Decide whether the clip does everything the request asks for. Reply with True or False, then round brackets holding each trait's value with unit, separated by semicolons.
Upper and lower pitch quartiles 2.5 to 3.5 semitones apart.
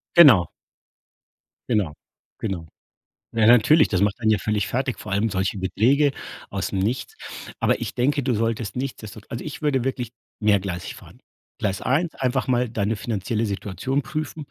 False (4.6 semitones)